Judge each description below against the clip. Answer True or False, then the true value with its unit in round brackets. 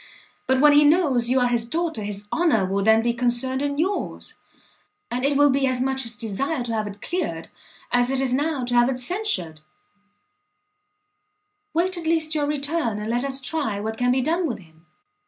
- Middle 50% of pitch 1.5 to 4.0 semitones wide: False (4.4 semitones)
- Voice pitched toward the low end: False (260 Hz)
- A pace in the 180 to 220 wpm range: True (200 wpm)